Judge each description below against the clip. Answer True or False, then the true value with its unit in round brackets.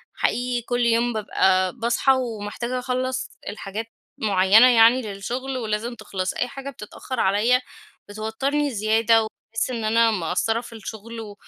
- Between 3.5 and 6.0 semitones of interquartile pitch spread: False (2.8 semitones)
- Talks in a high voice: True (230 Hz)